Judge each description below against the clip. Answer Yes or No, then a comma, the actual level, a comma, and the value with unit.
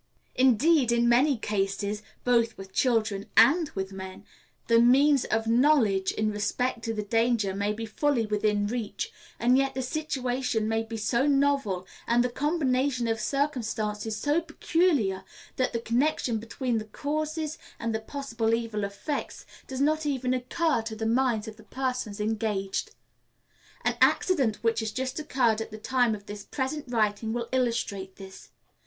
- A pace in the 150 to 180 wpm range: Yes, average, 160 wpm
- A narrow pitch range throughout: No, average, 3.7 semitones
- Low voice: No, high, 235 Hz